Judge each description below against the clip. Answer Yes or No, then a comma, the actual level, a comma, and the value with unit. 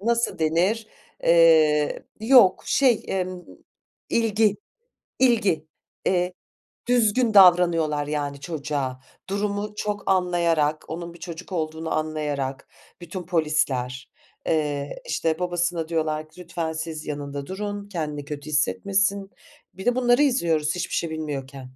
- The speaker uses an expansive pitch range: No, average, 4.6 semitones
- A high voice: No, medium, 165 Hz